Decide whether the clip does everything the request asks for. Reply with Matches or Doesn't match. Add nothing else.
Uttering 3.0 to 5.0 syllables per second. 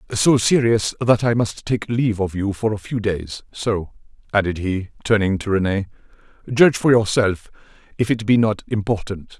Matches